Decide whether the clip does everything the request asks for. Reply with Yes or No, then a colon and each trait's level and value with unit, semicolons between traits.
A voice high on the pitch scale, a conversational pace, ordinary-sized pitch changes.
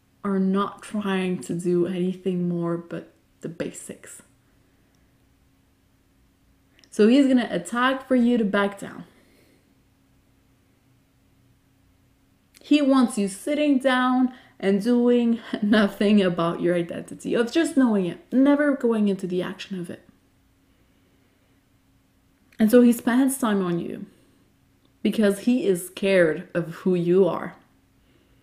No: high, 205 Hz; slow, 120 wpm; average, 5.0 semitones